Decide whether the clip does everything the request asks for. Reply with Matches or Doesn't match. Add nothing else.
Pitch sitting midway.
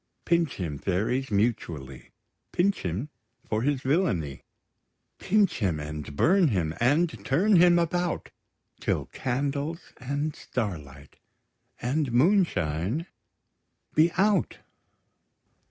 Doesn't match